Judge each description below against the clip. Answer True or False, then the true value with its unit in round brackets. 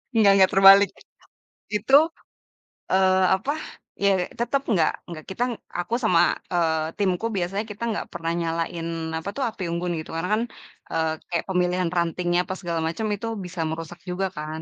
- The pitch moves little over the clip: False (3.0 semitones)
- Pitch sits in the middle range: True (180 Hz)